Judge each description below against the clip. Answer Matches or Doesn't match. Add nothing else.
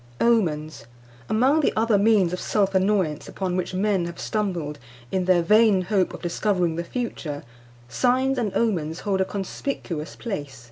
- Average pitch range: Matches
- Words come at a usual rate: Matches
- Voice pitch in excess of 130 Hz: Matches